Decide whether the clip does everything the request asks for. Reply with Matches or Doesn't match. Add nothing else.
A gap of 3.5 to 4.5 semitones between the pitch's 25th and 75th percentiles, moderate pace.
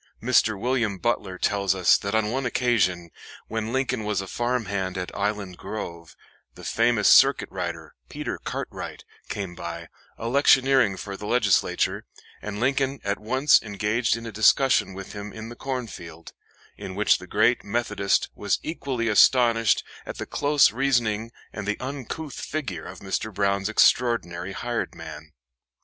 Matches